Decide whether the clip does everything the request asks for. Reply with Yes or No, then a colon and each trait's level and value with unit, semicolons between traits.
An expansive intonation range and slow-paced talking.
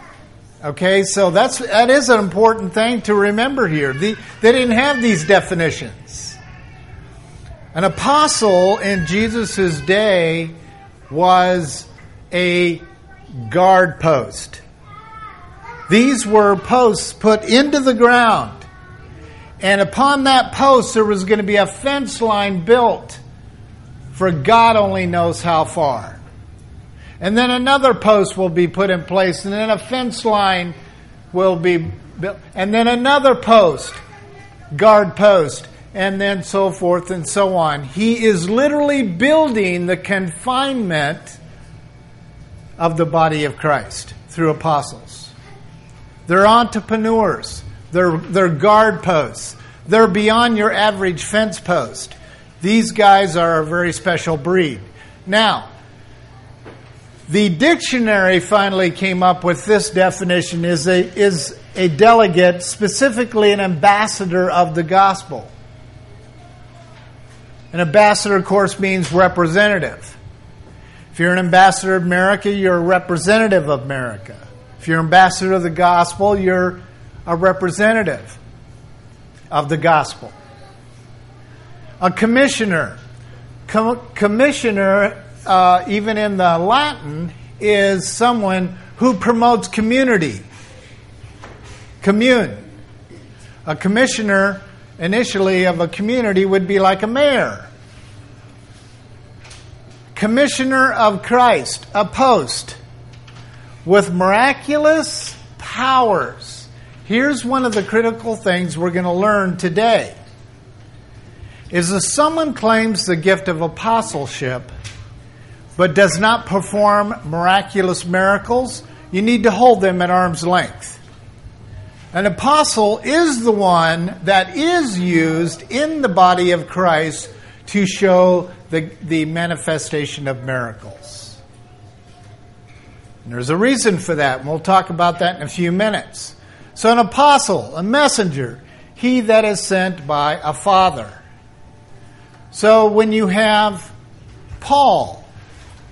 Yes: wide, 8.8 semitones; slow, 115 wpm